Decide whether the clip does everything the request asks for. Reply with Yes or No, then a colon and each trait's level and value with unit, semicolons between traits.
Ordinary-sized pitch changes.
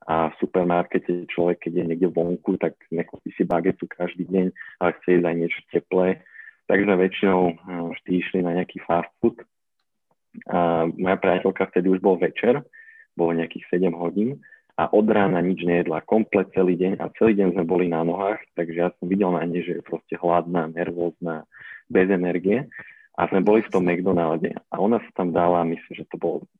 No: narrow, 1.5 semitones